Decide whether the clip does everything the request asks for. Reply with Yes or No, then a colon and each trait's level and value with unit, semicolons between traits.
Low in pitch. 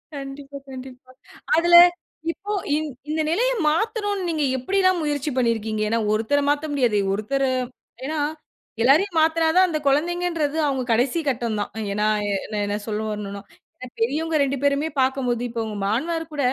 No: very high, 280 Hz